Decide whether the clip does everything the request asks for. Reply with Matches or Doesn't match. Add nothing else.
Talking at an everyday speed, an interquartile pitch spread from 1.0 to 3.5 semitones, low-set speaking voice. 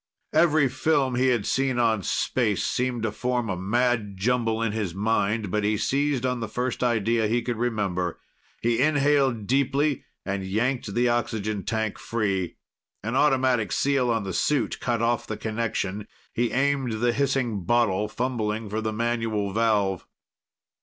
Matches